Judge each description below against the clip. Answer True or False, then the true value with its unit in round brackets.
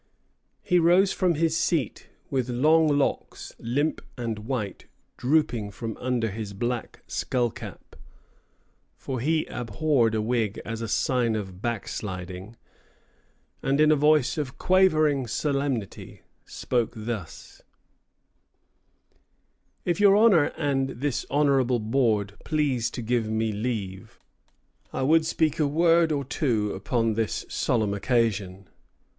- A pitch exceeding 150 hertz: False (125 Hz)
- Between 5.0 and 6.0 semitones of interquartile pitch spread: True (5.3 semitones)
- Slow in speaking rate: True (120 wpm)